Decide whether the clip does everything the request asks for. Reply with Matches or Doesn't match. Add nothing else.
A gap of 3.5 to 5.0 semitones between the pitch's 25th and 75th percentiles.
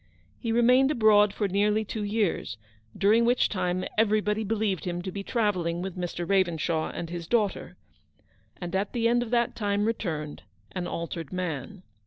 Matches